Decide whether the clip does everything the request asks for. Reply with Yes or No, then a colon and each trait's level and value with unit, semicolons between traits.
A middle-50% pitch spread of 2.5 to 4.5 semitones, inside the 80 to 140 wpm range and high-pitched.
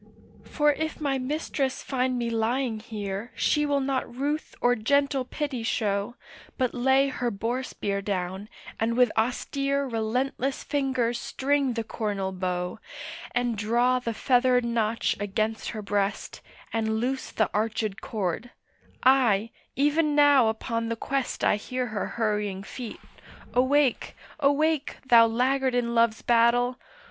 Yes: average, 3.5 semitones; slow, 135 wpm; high, 240 Hz